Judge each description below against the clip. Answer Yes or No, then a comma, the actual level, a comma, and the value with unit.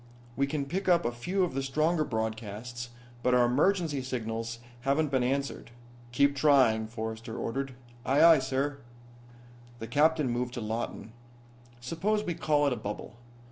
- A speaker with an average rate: Yes, average, 155 wpm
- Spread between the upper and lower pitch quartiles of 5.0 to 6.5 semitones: No, average, 4.1 semitones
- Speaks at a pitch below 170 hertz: Yes, low, 135 Hz